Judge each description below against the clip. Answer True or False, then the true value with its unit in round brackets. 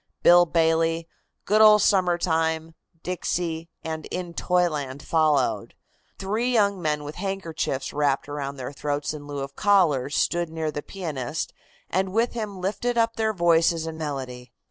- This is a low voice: False (165 Hz)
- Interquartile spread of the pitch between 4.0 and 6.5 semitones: True (4.3 semitones)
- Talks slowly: False (150 wpm)